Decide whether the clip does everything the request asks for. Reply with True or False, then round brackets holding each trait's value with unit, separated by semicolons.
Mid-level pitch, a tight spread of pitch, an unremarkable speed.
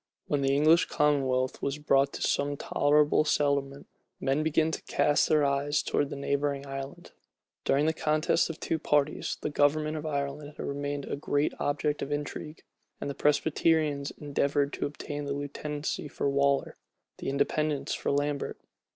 True (145 Hz; 1.2 semitones; 165 wpm)